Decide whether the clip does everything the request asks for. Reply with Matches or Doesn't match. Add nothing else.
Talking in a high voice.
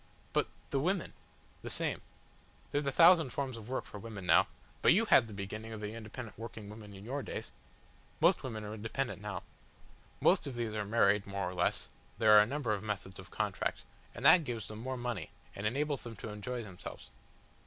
Doesn't match